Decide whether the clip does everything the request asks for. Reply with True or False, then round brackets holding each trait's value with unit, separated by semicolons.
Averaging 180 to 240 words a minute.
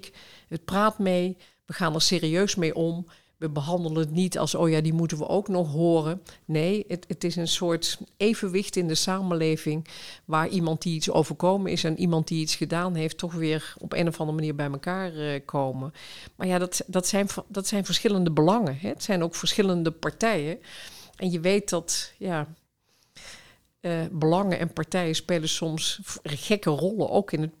True (185 wpm)